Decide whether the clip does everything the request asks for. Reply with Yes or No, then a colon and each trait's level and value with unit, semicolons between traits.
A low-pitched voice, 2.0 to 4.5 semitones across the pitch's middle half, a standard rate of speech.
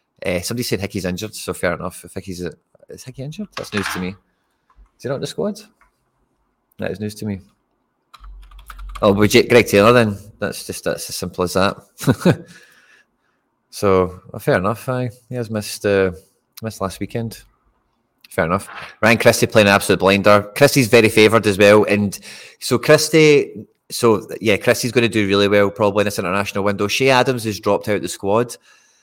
Yes: low, 105 Hz; average, 3.6 semitones; average, 185 wpm